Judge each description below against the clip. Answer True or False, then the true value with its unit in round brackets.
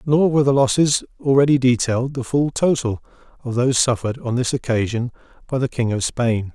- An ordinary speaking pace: True (185 wpm)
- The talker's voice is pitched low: True (125 Hz)